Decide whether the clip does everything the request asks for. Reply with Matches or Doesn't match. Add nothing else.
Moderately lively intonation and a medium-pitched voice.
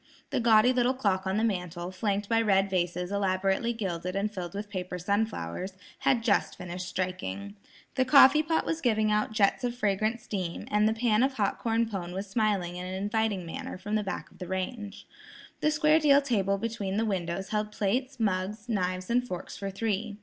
Doesn't match